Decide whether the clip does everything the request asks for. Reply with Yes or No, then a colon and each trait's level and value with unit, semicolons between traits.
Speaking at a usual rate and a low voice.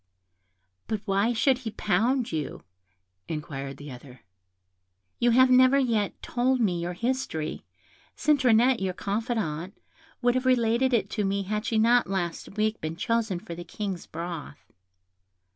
No: average, 145 wpm; high, 215 Hz